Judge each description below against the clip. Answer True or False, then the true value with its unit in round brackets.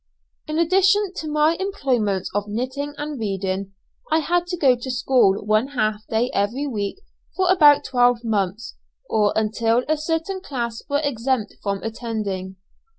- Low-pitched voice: False (245 Hz)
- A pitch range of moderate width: False (6.1 semitones)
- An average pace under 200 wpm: True (155 wpm)